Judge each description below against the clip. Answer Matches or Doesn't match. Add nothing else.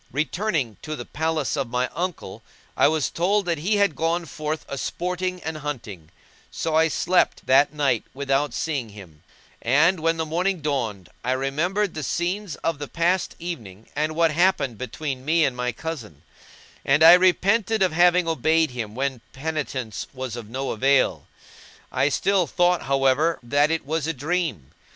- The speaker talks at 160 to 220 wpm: Matches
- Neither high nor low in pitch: Matches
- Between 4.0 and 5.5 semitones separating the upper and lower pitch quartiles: Matches